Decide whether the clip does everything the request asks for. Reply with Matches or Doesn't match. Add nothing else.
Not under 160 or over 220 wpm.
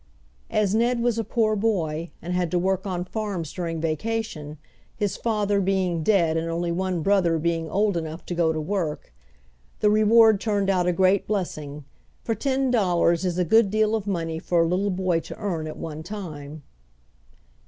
Matches